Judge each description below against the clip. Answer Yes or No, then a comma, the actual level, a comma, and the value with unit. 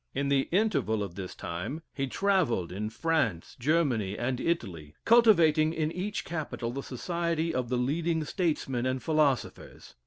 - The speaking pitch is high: No, medium, 140 Hz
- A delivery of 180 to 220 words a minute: No, average, 150 wpm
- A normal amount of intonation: No, wide, 6.1 semitones